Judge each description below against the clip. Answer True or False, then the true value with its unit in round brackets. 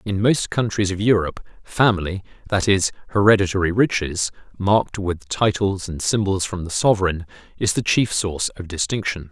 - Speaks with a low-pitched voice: True (100 Hz)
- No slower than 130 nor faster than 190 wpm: True (155 wpm)